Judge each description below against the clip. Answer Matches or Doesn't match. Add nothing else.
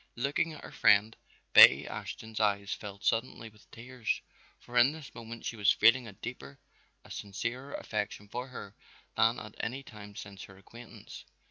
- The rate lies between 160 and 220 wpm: Matches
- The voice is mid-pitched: Doesn't match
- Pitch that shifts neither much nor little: Matches